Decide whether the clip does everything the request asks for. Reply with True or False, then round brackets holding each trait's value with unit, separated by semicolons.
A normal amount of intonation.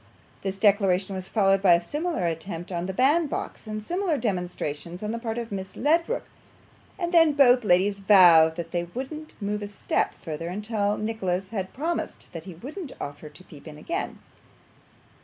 False (5.7 semitones)